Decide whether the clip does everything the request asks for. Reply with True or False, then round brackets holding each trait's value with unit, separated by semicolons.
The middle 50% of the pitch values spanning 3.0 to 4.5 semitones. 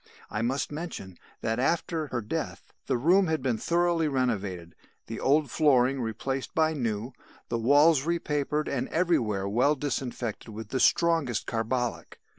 False (5.2 semitones)